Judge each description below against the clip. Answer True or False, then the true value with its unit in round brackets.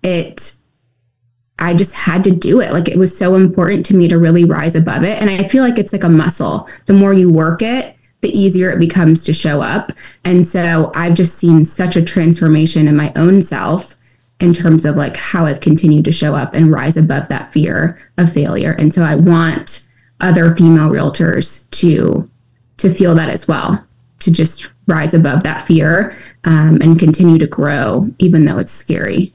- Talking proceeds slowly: False (195 wpm)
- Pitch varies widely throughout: False (2.7 semitones)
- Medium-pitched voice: True (165 Hz)